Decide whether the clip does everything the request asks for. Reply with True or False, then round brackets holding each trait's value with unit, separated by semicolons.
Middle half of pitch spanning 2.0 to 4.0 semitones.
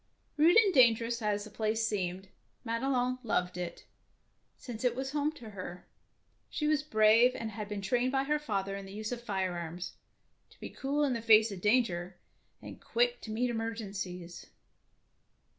False (4.4 semitones)